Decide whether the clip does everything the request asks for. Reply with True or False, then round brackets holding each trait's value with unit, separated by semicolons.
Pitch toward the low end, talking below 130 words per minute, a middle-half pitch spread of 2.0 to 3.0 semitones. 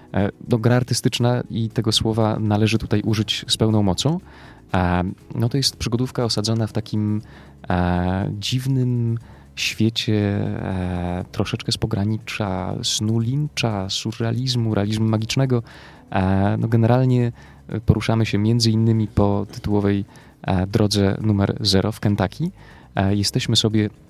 True (110 Hz; 110 wpm; 2.7 semitones)